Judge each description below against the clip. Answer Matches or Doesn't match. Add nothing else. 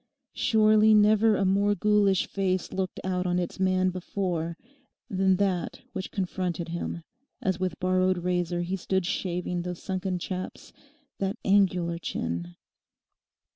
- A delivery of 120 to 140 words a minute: Matches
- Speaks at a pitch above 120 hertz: Matches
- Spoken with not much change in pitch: Matches